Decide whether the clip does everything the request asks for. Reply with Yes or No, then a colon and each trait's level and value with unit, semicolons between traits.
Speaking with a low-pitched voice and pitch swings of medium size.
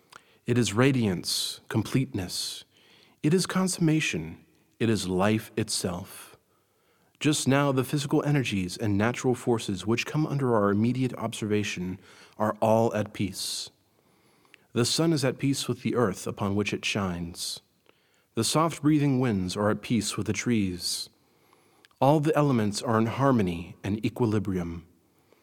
Yes: low, 115 Hz; average, 4.5 semitones